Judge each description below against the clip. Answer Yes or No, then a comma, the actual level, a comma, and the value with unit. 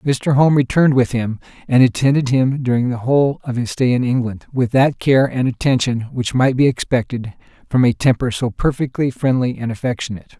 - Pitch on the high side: No, low, 125 Hz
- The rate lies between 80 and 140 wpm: No, average, 190 wpm